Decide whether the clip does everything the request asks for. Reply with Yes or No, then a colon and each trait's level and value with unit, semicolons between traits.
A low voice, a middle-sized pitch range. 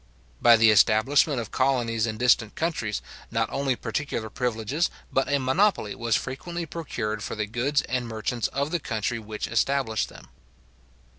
Yes: low, 120 Hz; average, 4.1 semitones